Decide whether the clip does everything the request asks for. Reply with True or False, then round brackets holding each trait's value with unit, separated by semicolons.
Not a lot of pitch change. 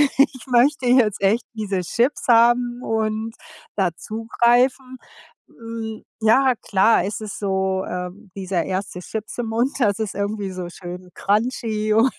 False (3.6 semitones)